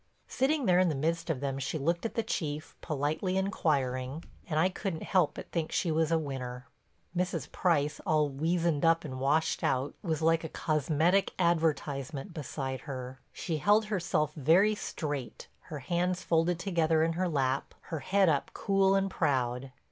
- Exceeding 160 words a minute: Yes, average, 170 wpm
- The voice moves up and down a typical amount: Yes, average, 3.9 semitones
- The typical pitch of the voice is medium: Yes, medium, 160 Hz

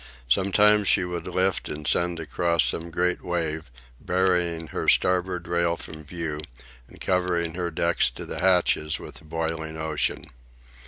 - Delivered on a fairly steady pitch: Yes, narrow, 2.0 semitones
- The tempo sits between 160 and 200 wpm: No, average, 150 wpm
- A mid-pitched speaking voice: No, very low, 85 Hz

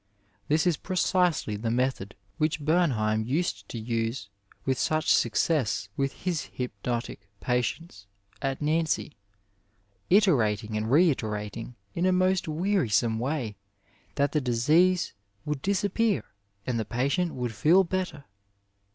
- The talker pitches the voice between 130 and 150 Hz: Yes, low, 135 Hz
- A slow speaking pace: Yes, slow, 120 wpm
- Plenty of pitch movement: Yes, wide, 7.2 semitones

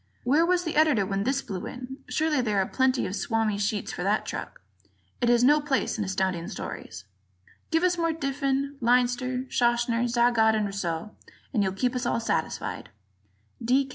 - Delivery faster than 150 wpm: Yes, average, 180 wpm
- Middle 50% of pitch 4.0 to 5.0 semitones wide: Yes, average, 4.4 semitones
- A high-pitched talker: Yes, high, 245 Hz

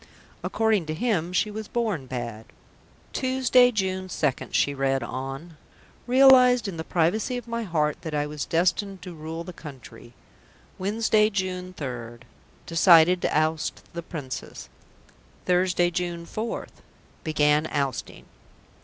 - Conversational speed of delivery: No, slow, 130 wpm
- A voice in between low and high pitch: Yes, medium, 170 Hz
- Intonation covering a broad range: Yes, wide, 5.8 semitones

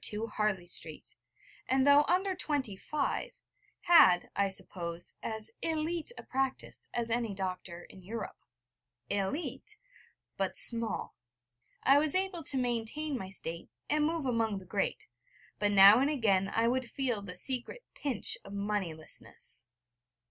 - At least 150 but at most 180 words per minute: No, average, 140 wpm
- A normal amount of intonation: No, wide, 6.5 semitones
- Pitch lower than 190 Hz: No, high, 230 Hz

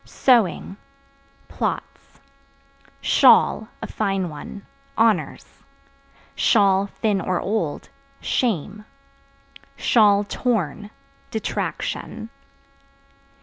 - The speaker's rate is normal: No, slow, 60 wpm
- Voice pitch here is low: No, high, 200 Hz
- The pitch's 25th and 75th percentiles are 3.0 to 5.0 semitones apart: No, narrow, 2.6 semitones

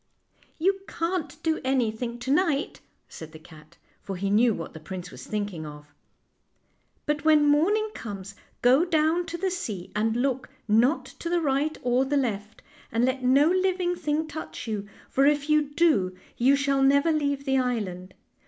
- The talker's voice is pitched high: Yes, very high, 270 Hz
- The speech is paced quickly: No, average, 180 wpm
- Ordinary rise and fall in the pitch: No, wide, 6.7 semitones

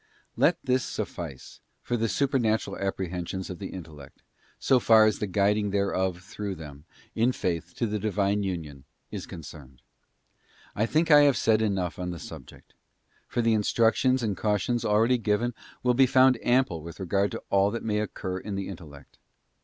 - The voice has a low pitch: Yes, low, 105 Hz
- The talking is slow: No, average, 170 wpm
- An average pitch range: Yes, average, 4.2 semitones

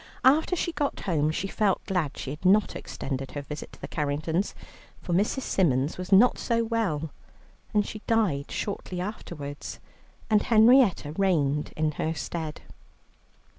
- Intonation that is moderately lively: No, wide, 6.3 semitones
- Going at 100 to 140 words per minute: No, average, 150 wpm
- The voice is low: No, medium, 180 Hz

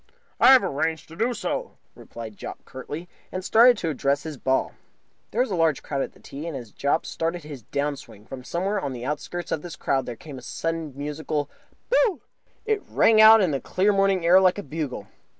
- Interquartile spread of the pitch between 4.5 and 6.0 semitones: Yes, wide, 5.6 semitones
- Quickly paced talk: Yes, fast, 215 wpm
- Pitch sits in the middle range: Yes, medium, 160 Hz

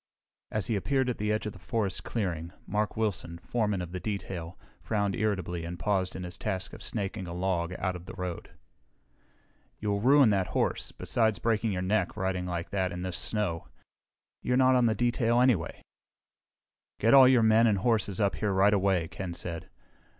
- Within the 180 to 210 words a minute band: Yes, average, 185 wpm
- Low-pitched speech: Yes, low, 100 Hz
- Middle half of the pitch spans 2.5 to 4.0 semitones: Yes, average, 3.4 semitones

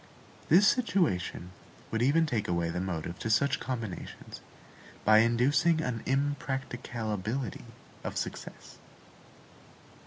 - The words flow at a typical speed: No, slow, 100 wpm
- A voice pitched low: Yes, low, 120 Hz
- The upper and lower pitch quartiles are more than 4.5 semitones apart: Yes, average, 5.1 semitones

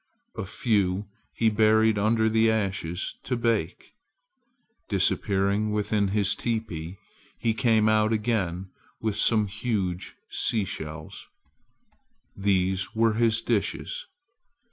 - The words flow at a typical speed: No, slow, 100 wpm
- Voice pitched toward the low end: Yes, low, 105 Hz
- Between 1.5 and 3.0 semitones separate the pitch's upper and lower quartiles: Yes, narrow, 2.5 semitones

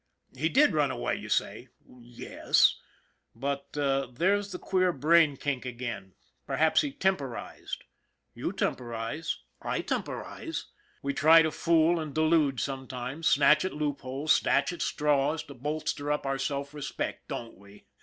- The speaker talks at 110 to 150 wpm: Yes, average, 140 wpm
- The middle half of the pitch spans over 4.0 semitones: No, average, 3.5 semitones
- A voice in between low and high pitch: Yes, medium, 145 Hz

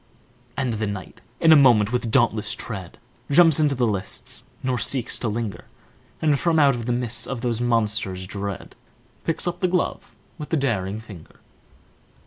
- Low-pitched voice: Yes, low, 120 Hz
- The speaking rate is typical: Yes, average, 165 wpm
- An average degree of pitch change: Yes, average, 4.8 semitones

